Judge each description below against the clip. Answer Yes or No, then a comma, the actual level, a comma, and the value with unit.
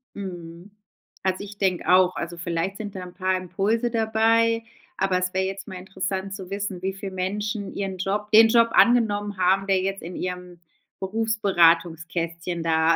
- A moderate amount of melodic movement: No, narrow, 2.3 semitones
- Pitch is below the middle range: No, high, 190 Hz